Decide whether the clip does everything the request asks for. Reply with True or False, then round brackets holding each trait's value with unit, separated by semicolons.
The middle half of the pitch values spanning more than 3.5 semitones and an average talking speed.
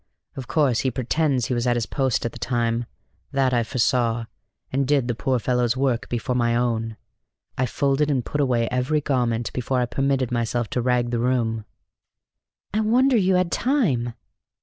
False (2.5 semitones; 180 wpm)